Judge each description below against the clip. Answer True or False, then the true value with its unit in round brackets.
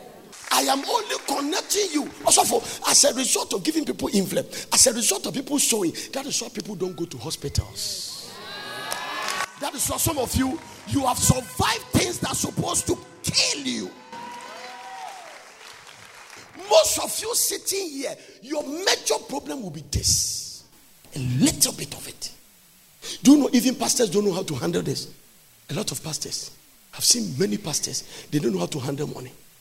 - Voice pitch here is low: False (245 Hz)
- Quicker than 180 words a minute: False (175 wpm)